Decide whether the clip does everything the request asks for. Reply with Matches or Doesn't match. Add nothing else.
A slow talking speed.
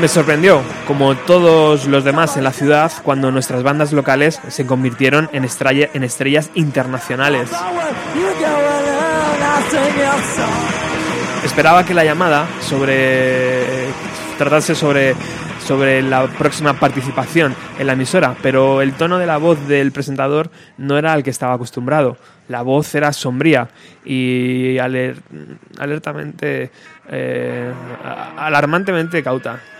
Matches